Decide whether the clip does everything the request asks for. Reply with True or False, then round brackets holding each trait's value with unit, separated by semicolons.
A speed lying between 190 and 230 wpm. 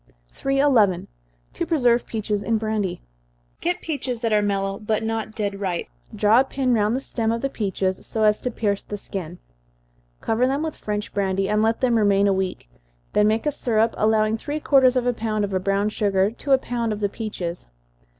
True (200 wpm)